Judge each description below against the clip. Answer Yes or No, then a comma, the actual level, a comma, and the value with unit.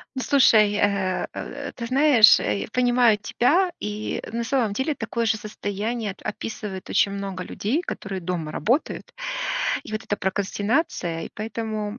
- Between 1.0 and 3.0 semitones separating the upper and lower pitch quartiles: No, average, 3.5 semitones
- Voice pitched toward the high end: Yes, high, 215 Hz